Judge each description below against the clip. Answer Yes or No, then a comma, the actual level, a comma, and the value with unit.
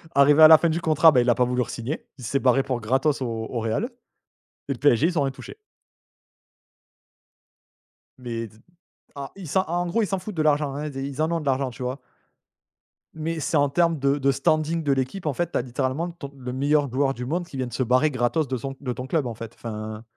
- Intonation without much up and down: No, average, 3.8 semitones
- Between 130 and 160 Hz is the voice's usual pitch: Yes, medium, 140 Hz